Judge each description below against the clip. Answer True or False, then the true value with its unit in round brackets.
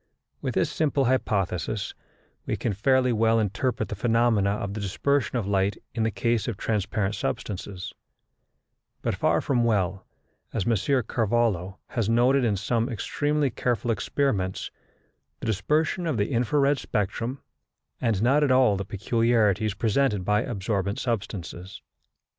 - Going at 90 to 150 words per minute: True (140 wpm)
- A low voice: True (110 Hz)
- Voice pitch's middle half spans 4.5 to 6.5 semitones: False (3.9 semitones)